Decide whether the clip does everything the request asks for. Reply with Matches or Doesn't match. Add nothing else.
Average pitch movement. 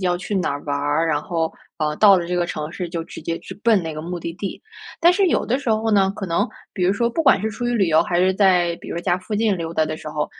Matches